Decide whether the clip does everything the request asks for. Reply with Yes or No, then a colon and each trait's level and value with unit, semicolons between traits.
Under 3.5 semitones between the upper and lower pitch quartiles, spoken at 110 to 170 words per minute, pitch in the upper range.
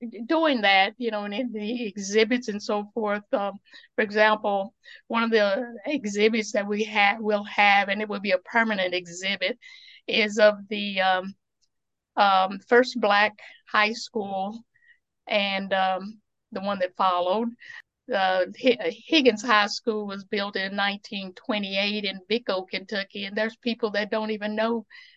Yes: narrow, 2.6 semitones; average, 155 wpm; high, 210 Hz